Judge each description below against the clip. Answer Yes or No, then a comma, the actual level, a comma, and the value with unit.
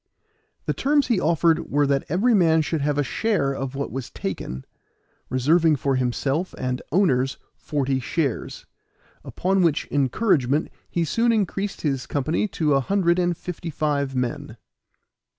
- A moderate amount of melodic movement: Yes, average, 4.7 semitones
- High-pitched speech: No, medium, 150 Hz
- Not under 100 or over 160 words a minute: Yes, average, 150 wpm